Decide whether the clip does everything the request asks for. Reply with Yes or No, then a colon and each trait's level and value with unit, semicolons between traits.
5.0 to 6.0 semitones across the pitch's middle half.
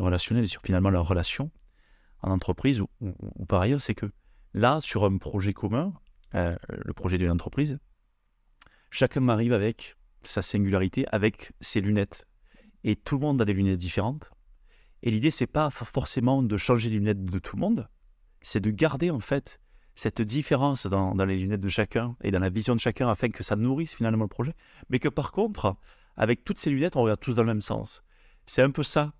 Yes: wide, 5.4 semitones